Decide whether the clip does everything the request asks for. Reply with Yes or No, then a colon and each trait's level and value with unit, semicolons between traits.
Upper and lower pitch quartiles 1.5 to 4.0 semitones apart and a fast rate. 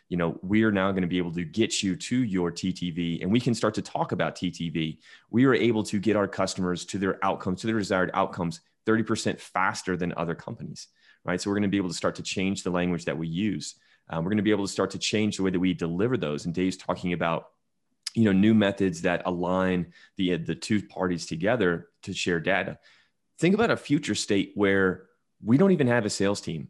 Yes: average, 3.1 semitones; fast, 235 wpm